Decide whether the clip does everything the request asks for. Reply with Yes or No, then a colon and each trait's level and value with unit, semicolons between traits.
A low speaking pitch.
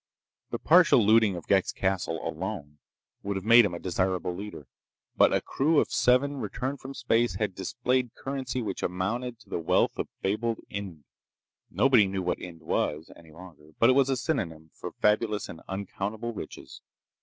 Yes: low, 105 Hz